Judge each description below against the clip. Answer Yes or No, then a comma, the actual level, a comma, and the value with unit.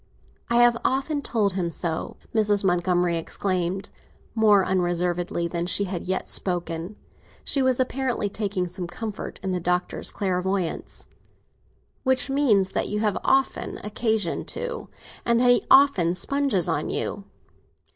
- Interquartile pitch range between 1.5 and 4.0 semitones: No, average, 4.8 semitones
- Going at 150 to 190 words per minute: No, slow, 135 wpm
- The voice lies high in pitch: Yes, high, 195 Hz